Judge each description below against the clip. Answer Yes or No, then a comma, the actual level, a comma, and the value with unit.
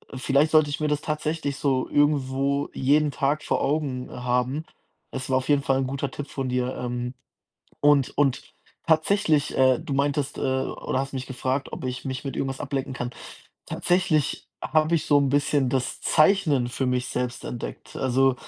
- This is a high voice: No, low, 135 Hz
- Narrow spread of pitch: Yes, narrow, 2.1 semitones